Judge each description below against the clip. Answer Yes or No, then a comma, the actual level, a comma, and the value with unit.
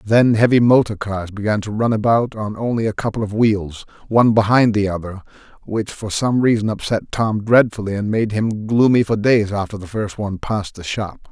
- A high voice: No, low, 105 Hz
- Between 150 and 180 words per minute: No, average, 200 wpm